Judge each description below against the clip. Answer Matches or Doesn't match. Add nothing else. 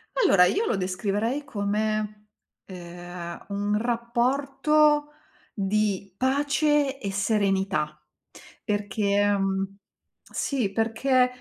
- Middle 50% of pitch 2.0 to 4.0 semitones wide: Doesn't match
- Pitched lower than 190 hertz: Doesn't match